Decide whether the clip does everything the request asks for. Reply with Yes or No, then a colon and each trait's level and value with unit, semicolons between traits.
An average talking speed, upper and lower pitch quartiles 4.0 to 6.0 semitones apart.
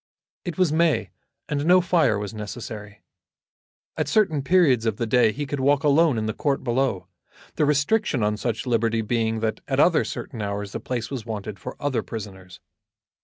Yes: average, 180 wpm; average, 5.1 semitones